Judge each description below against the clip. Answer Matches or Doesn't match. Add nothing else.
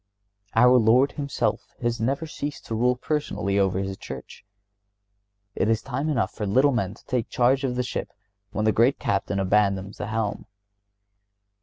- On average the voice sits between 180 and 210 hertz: Doesn't match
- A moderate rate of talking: Matches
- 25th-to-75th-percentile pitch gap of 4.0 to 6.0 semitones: Matches